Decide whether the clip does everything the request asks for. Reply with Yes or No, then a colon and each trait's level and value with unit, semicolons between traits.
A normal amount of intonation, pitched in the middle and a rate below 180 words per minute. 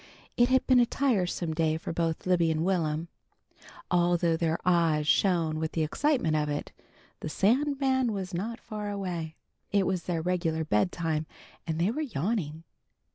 Yes: average, 4.3 semitones; medium, 175 Hz; average, 160 wpm